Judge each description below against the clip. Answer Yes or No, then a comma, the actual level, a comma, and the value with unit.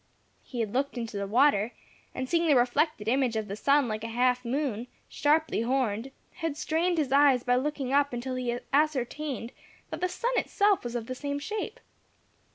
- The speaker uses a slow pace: No, average, 185 wpm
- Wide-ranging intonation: No, average, 3.9 semitones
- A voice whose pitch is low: No, very high, 260 Hz